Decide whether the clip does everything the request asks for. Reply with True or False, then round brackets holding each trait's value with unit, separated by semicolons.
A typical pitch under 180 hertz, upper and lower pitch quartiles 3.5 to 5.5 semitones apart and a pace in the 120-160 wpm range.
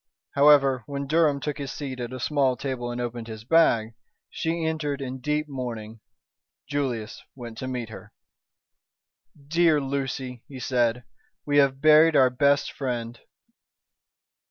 False (135 Hz; 3.1 semitones; 140 wpm)